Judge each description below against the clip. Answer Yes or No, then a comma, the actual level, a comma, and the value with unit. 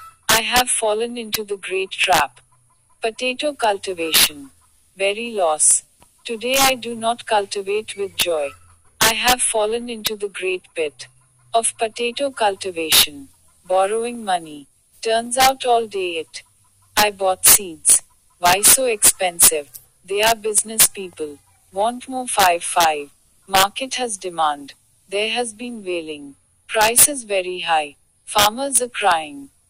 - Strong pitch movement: Yes, wide, 6.7 semitones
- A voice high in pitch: Yes, high, 205 Hz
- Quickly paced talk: Yes, fast, 130 wpm